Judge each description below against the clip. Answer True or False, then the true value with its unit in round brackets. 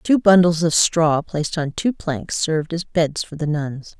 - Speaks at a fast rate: True (210 wpm)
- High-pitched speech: False (165 Hz)